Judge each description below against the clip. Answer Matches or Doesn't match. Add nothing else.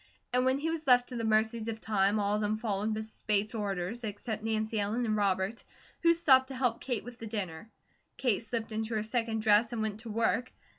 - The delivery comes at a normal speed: Doesn't match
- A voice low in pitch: Doesn't match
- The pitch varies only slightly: Matches